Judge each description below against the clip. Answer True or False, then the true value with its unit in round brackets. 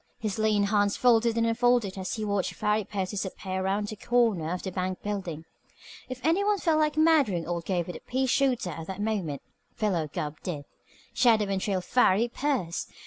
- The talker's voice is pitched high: True (205 Hz)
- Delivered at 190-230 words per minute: True (195 wpm)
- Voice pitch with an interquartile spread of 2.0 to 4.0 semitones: False (4.5 semitones)